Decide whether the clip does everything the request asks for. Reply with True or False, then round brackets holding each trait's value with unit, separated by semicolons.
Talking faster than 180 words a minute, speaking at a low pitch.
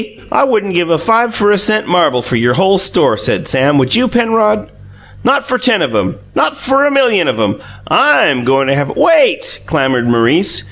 False (205 wpm; 195 Hz)